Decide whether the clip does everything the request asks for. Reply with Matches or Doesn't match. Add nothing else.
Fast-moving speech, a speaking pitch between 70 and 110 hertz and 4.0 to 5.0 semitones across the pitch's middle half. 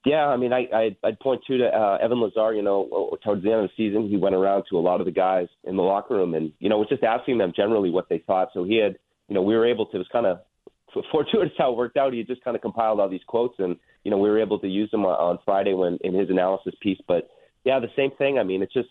Doesn't match